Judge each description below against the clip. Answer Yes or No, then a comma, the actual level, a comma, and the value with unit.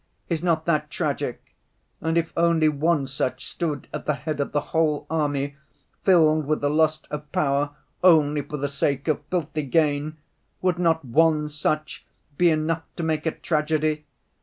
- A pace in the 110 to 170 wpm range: Yes, average, 160 wpm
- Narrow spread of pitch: Yes, narrow, 1.9 semitones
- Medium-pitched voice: Yes, medium, 155 Hz